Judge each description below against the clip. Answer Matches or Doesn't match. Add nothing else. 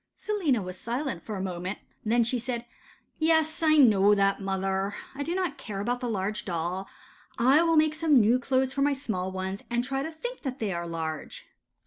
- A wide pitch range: Matches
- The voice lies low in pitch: Doesn't match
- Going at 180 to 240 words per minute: Matches